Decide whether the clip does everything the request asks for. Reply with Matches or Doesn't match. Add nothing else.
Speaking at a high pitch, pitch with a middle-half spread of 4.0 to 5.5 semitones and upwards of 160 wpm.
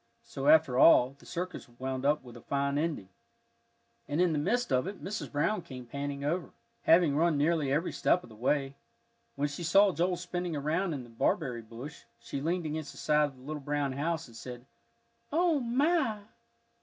Doesn't match